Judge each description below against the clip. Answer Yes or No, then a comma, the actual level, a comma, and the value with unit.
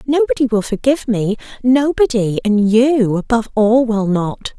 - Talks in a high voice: Yes, high, 230 Hz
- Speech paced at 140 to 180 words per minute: Yes, average, 145 wpm